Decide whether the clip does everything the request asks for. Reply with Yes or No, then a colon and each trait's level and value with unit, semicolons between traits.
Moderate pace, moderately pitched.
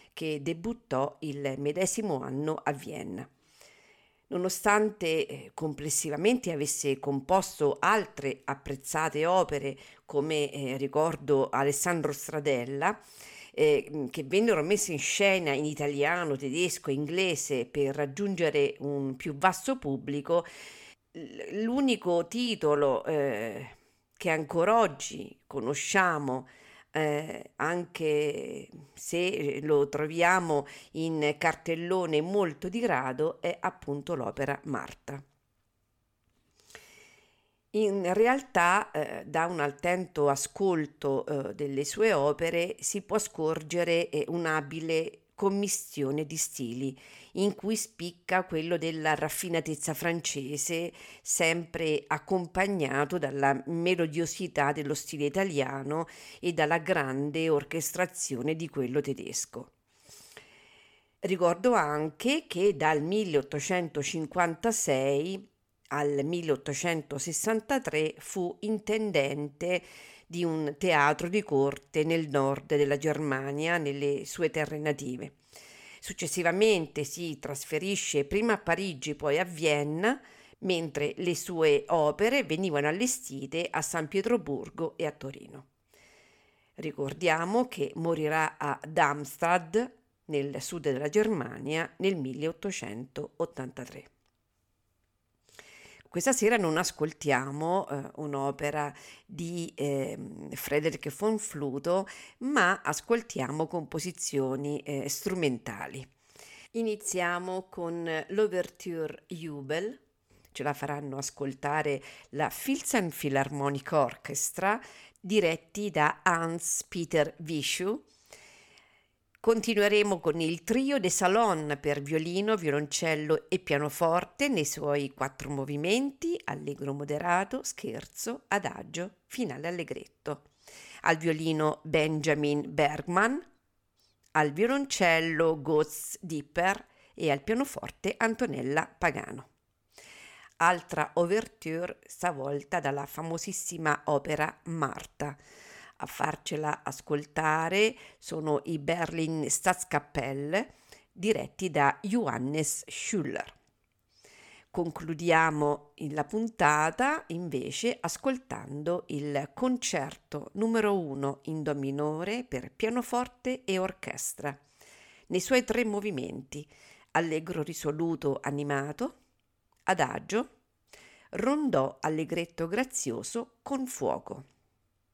No: slow, 90 wpm; medium, 160 Hz